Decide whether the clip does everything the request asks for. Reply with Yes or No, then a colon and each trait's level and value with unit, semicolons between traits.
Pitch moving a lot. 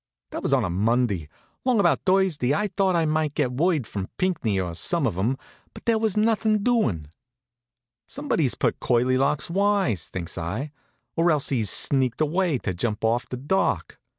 Yes: wide, 8.7 semitones